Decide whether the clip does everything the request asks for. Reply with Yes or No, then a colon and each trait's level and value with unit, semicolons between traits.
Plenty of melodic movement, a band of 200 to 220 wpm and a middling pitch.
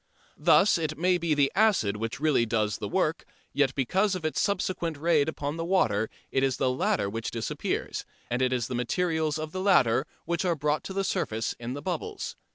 Yes: wide, 6.1 semitones; fast, 205 wpm; medium, 150 Hz